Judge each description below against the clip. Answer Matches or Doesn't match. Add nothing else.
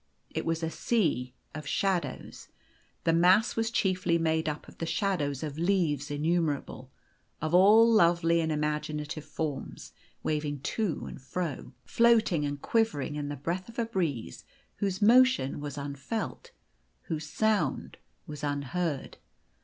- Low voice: Doesn't match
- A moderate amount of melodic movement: Matches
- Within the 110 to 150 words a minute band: Matches